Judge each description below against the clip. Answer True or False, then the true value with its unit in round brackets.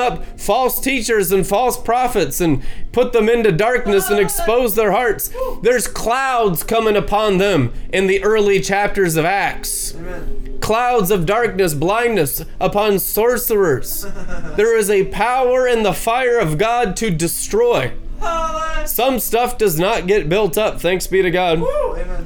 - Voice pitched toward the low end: False (215 Hz)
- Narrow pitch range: False (4.3 semitones)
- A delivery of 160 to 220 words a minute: False (145 wpm)